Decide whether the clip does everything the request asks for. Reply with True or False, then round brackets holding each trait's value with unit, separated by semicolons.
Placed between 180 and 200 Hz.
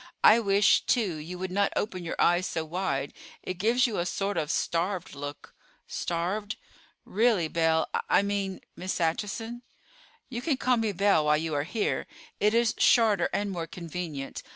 True (185 Hz)